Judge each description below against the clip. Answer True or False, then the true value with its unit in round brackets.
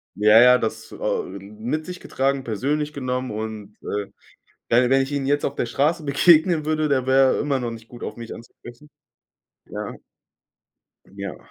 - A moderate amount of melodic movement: True (4.3 semitones)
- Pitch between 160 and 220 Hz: False (130 Hz)